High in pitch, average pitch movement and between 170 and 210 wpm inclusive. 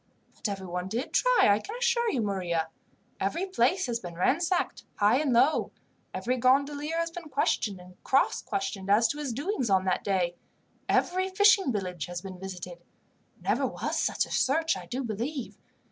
No: high, 240 Hz; wide, 8.7 semitones; average, 175 wpm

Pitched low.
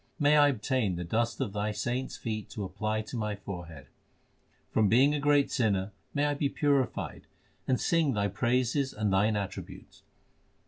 Yes: low, 115 Hz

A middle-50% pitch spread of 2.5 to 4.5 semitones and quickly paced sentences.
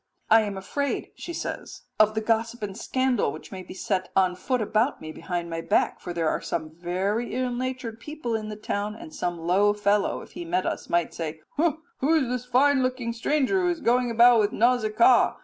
No: average, 5.2 semitones; fast, 210 wpm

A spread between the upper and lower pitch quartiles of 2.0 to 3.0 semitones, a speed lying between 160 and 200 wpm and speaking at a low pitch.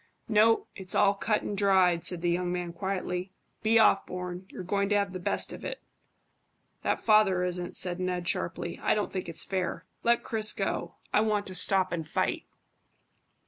No: narrow, 2.5 semitones; average, 185 wpm; high, 190 Hz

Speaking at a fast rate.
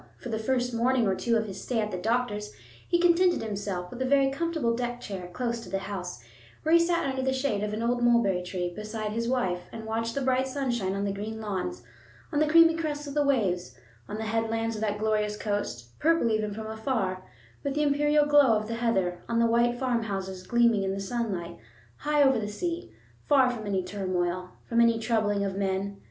Yes: fast, 215 wpm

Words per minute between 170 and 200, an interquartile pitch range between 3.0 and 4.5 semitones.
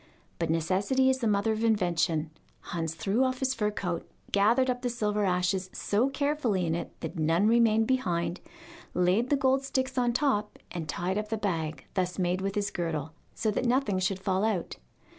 No: average, 190 wpm; average, 5.2 semitones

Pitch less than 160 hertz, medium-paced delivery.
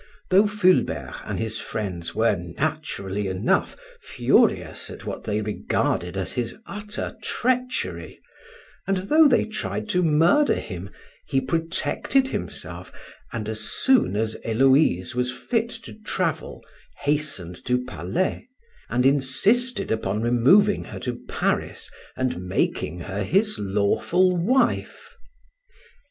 No: low, 135 Hz; slow, 120 wpm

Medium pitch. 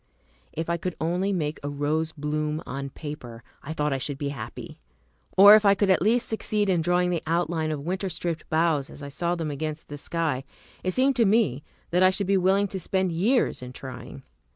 Yes: medium, 165 Hz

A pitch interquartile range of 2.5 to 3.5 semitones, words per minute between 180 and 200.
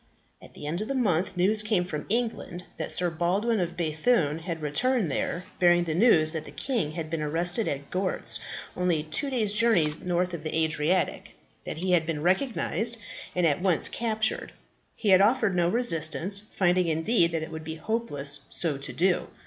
No: average, 4.9 semitones; average, 190 wpm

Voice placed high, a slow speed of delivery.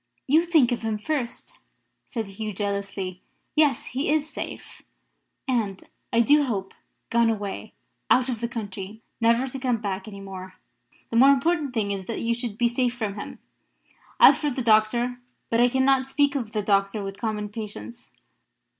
No: high, 230 Hz; average, 170 wpm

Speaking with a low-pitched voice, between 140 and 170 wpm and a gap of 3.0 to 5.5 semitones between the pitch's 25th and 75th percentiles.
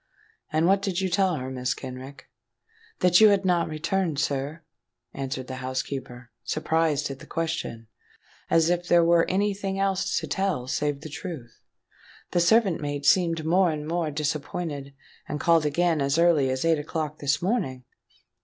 No: medium, 160 Hz; average, 165 wpm; average, 4.2 semitones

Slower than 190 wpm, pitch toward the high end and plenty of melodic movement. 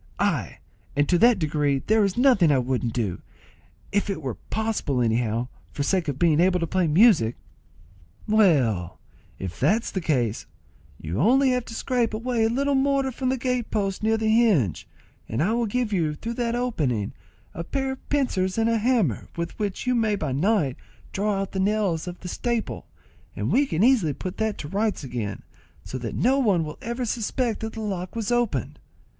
No: average, 195 wpm; high, 200 Hz; wide, 7.7 semitones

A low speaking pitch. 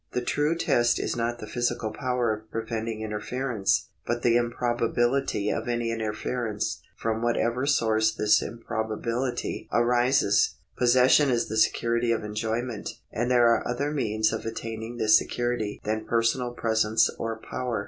Yes: low, 115 Hz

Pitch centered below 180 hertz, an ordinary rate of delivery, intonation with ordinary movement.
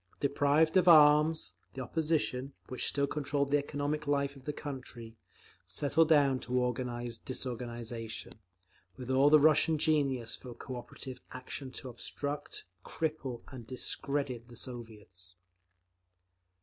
No: low, 135 Hz; slow, 120 wpm; average, 3.1 semitones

